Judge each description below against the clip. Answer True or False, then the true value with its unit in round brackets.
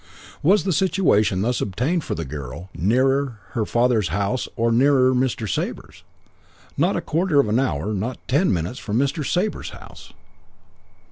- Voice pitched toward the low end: True (125 Hz)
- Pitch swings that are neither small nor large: False (5.7 semitones)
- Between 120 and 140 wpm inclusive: False (155 wpm)